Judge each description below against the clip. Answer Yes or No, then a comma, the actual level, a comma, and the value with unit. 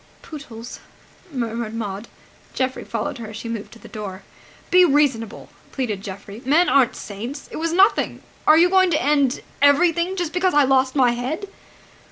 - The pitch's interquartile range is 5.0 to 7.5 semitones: Yes, wide, 5.6 semitones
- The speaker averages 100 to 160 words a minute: No, average, 170 wpm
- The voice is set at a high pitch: Yes, very high, 260 Hz